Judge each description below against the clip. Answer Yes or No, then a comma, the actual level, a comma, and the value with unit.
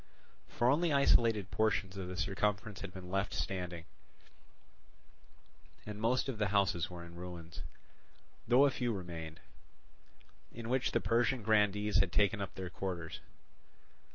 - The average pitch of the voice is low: Yes, low, 100 Hz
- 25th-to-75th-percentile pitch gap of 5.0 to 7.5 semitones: No, average, 4.0 semitones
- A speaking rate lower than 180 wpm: Yes, average, 140 wpm